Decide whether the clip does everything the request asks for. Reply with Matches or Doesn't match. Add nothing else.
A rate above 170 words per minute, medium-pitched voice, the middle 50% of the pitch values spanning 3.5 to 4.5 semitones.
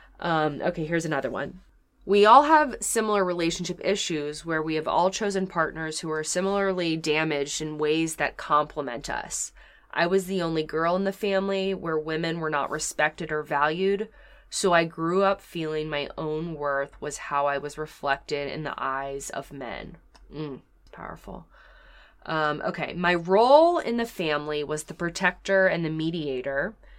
Doesn't match